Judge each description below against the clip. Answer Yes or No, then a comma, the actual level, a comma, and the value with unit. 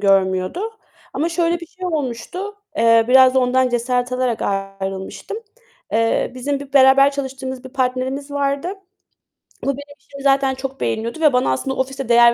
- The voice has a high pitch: Yes, very high, 265 Hz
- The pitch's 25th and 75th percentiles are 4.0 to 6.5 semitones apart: No, average, 2.9 semitones